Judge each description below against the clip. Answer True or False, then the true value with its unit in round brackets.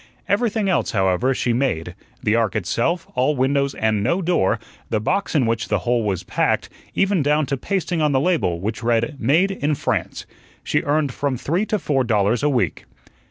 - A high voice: False (135 Hz)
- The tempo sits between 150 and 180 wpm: False (190 wpm)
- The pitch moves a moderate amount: False (6.1 semitones)